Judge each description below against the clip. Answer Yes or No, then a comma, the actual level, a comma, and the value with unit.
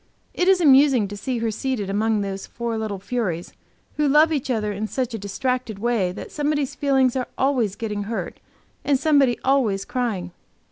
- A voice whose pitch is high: Yes, high, 240 Hz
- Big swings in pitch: No, average, 4.7 semitones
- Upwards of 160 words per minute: Yes, average, 180 wpm